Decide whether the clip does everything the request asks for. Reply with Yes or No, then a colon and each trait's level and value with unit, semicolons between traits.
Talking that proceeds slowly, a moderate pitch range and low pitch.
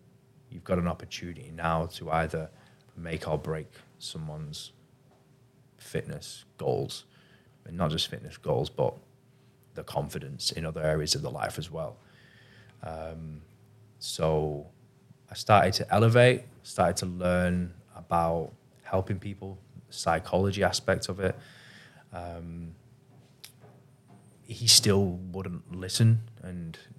No: slow, 115 wpm; wide, 6.1 semitones; very low, 95 Hz